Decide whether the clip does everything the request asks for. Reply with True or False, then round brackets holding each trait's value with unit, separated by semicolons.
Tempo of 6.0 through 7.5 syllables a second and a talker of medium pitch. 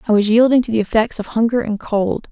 False (6.1 syllables/s; 225 Hz)